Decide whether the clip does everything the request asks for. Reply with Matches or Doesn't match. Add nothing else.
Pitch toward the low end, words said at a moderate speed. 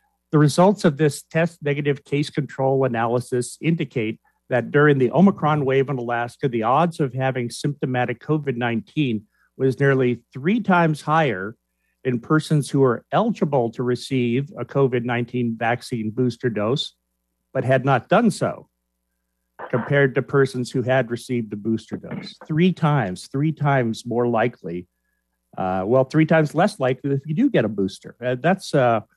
Matches